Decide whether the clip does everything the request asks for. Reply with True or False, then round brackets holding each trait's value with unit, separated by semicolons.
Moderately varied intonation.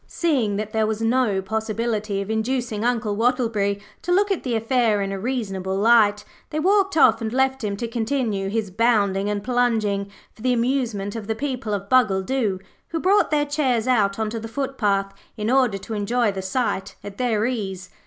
True (3.8 semitones)